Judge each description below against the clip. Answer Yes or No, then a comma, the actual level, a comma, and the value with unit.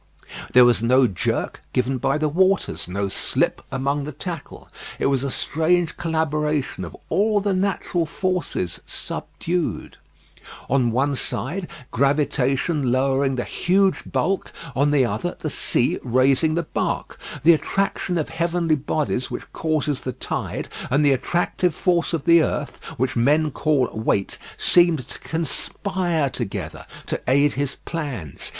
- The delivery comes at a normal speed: Yes, average, 145 wpm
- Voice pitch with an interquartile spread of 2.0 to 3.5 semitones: No, average, 4.5 semitones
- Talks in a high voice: No, medium, 145 Hz